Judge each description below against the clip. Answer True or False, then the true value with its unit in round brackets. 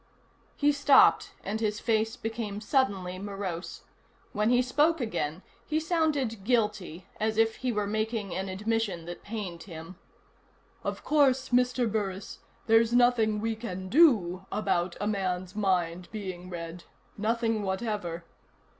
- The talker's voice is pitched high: True (210 Hz)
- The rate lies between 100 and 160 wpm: True (135 wpm)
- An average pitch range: True (3.9 semitones)